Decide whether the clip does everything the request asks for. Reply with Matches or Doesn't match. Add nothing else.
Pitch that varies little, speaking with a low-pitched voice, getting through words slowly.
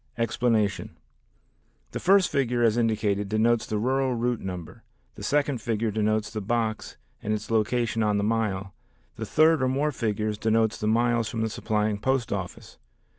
Doesn't match